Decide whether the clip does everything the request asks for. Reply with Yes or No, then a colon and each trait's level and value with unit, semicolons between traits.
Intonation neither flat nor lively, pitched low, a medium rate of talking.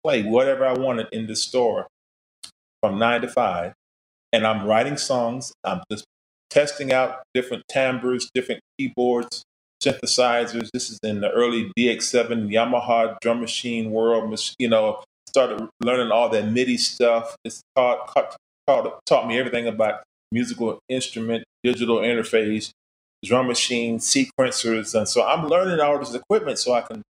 No: narrow, 2.1 semitones; low, 120 Hz; average, 150 wpm